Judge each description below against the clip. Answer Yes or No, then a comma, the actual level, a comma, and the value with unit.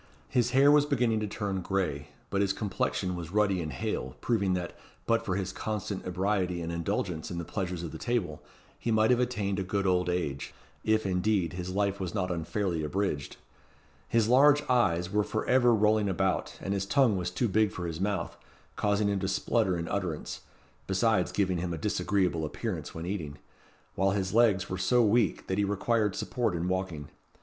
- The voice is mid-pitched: No, very low, 95 Hz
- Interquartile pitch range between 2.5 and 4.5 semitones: Yes, average, 3.2 semitones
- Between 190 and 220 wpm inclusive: Yes, average, 195 wpm